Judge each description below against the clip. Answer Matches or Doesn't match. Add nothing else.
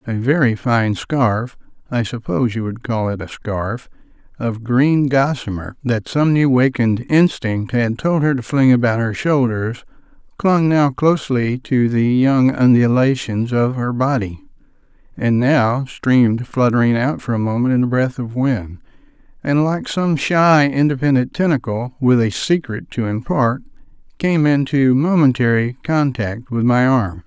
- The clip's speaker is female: Doesn't match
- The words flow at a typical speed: Matches